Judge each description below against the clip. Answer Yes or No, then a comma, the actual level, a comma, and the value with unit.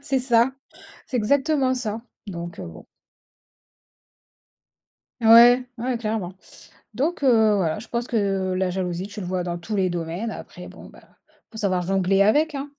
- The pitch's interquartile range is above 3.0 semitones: Yes, average, 5.0 semitones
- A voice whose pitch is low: No, high, 215 Hz